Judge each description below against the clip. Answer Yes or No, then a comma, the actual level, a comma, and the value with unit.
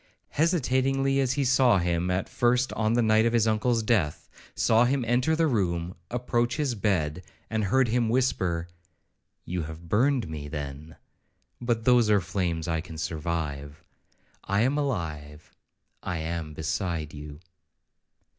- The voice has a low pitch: Yes, low, 105 Hz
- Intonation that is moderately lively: No, wide, 7.1 semitones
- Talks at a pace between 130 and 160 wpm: Yes, slow, 135 wpm